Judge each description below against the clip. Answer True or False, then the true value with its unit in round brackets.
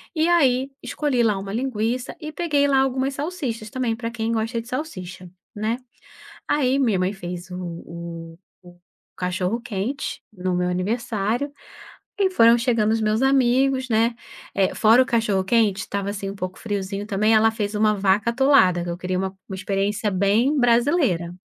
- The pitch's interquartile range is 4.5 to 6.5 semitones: True (4.9 semitones)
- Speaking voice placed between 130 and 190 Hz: False (220 Hz)